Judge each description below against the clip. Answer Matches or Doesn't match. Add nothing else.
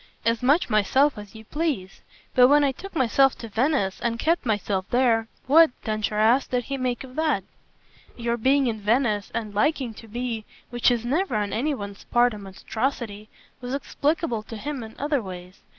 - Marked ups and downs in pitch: Doesn't match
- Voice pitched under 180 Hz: Doesn't match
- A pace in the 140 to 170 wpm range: Doesn't match